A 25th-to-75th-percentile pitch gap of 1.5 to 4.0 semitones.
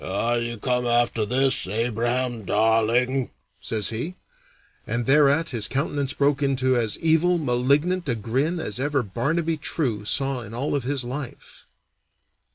Yes: average, 3.5 semitones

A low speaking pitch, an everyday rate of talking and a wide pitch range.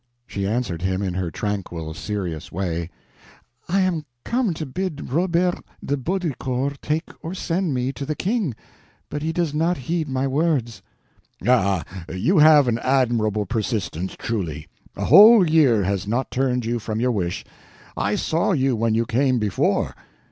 Yes: low, 125 Hz; average, 160 wpm; wide, 7.5 semitones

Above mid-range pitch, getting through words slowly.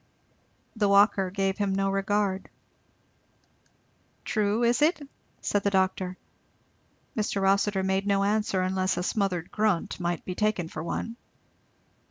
Yes: high, 195 Hz; slow, 130 wpm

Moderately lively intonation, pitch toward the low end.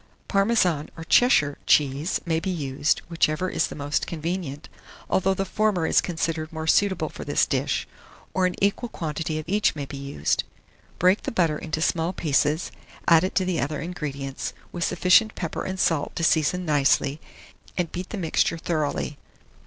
No: average, 3.4 semitones; medium, 165 Hz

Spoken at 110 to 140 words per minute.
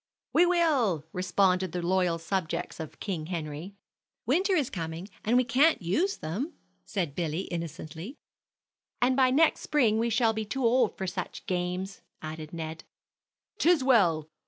No: average, 150 wpm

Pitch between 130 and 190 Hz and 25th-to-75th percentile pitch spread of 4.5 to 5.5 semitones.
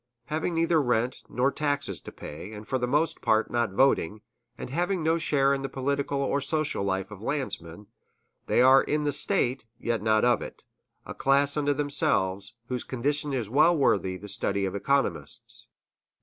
Yes: low, 135 Hz; average, 5.1 semitones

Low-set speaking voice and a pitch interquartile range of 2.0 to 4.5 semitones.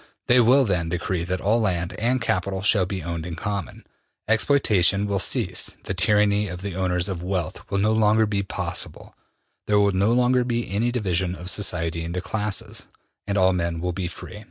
Yes: low, 100 Hz; average, 3.1 semitones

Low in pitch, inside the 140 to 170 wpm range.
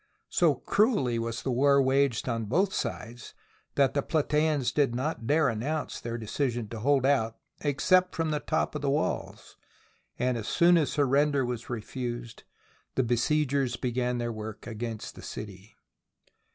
Yes: low, 130 Hz; average, 155 wpm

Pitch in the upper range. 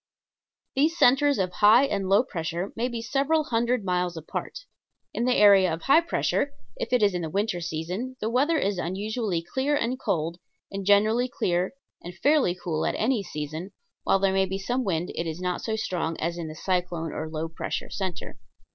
Yes: high, 195 Hz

